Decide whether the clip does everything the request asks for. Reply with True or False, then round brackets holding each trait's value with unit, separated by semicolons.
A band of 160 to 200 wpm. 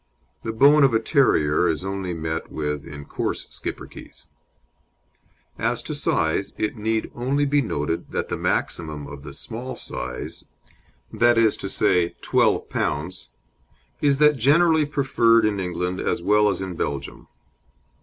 False (135 wpm)